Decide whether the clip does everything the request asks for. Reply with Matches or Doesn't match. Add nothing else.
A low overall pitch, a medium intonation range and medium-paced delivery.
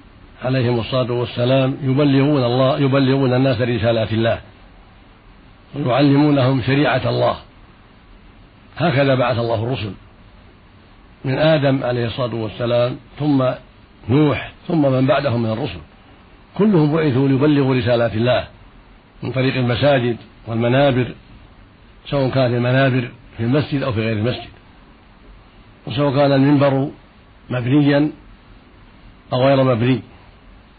Matches